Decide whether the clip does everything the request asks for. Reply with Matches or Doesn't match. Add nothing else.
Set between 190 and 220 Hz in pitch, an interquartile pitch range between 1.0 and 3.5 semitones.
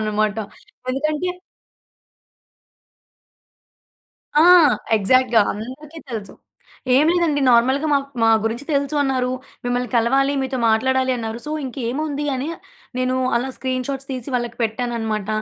Doesn't match